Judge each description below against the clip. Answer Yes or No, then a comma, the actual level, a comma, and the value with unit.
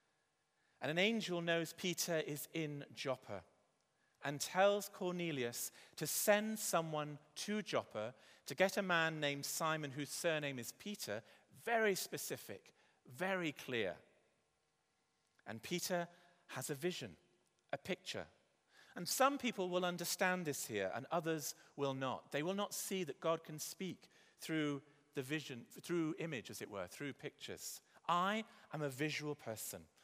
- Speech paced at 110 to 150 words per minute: Yes, average, 140 wpm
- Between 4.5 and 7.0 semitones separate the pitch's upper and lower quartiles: Yes, average, 4.8 semitones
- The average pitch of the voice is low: No, medium, 160 Hz